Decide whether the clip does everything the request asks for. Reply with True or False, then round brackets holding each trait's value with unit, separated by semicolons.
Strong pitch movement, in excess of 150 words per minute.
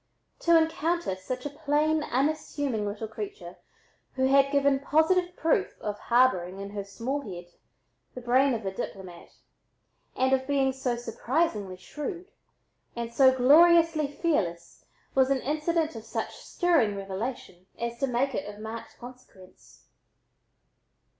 False (6.1 semitones; 135 wpm)